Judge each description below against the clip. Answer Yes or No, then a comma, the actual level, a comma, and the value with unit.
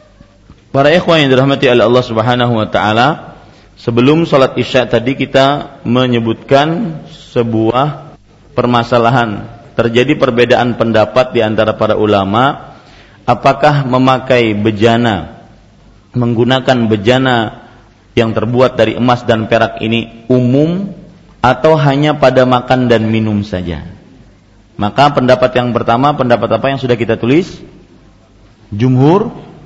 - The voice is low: Yes, low, 120 Hz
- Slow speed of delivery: No, average, 110 wpm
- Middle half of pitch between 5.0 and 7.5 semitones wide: No, average, 2.9 semitones